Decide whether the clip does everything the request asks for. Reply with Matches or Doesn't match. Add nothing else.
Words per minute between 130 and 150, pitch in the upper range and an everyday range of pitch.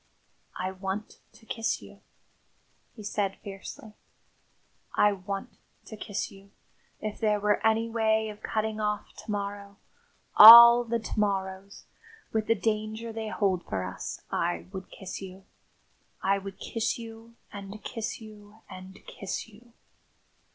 Doesn't match